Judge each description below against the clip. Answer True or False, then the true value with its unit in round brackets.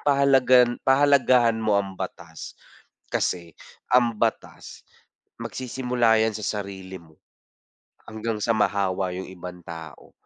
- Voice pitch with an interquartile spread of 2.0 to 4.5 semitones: False (5.1 semitones)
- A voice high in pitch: False (110 Hz)